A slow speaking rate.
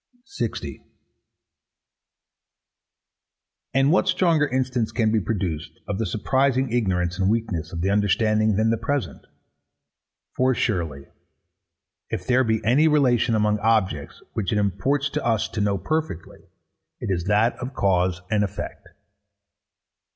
Yes: slow, 130 wpm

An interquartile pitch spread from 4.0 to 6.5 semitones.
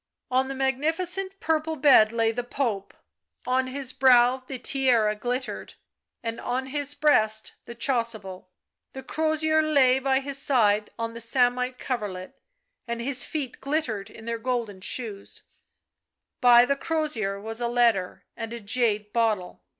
No: average, 3.3 semitones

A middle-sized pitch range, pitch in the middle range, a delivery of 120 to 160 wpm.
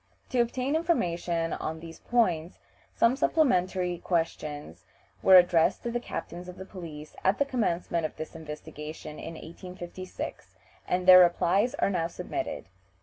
Yes: average, 4.0 semitones; medium, 180 Hz; average, 140 wpm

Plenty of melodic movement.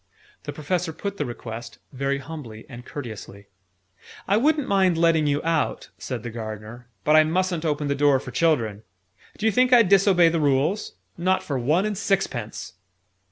Yes: wide, 7.1 semitones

